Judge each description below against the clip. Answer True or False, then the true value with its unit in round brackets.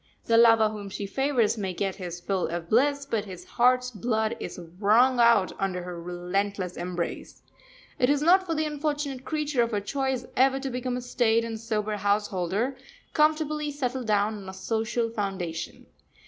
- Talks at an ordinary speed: True (175 wpm)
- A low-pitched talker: False (225 Hz)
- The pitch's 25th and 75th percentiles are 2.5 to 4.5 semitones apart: False (5.1 semitones)